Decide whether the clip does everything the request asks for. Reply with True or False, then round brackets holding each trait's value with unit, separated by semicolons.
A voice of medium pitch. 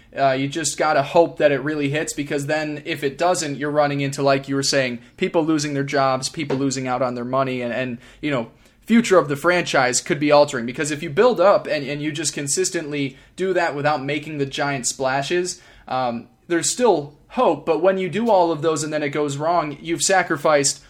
True (150 Hz)